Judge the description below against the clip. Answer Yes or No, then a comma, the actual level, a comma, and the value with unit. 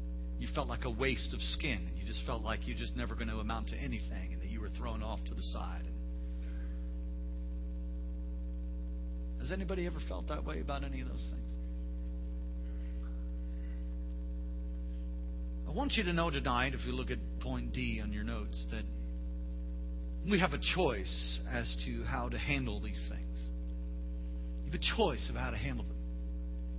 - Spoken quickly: No, average, 170 wpm